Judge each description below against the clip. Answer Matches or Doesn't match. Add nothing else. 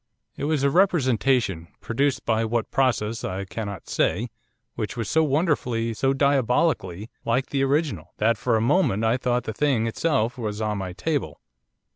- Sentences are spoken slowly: Doesn't match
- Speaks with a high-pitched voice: Doesn't match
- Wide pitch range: Doesn't match